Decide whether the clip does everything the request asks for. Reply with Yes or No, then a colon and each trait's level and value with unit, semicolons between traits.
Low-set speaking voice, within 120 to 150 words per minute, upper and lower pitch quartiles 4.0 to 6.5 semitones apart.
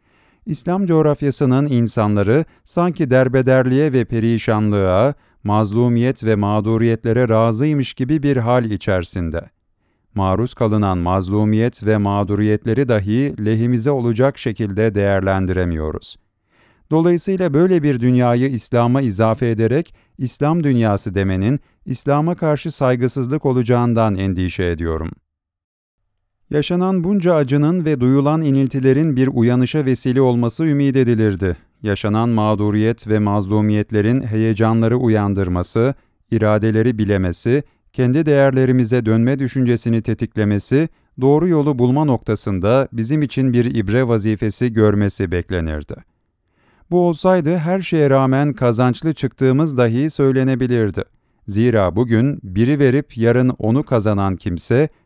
No: low, 120 Hz; average, 100 wpm; average, 4.4 semitones